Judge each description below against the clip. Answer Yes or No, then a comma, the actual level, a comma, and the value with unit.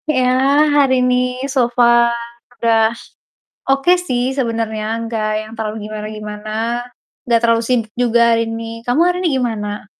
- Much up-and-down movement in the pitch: No, narrow, 2.4 semitones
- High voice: Yes, high, 235 Hz